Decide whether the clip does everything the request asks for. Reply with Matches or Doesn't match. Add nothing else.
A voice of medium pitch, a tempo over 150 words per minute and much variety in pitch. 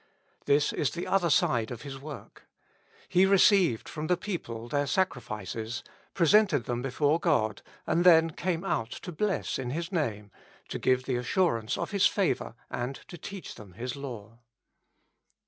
Matches